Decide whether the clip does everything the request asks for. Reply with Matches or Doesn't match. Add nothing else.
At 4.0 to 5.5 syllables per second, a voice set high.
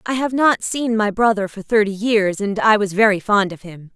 Matches